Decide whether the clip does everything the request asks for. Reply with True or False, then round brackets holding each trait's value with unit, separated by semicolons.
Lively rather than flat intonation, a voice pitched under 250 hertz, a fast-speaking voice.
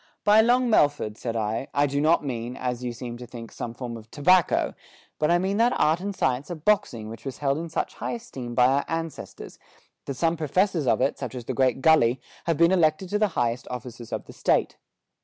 True (5.8 semitones; 140 Hz; 230 wpm)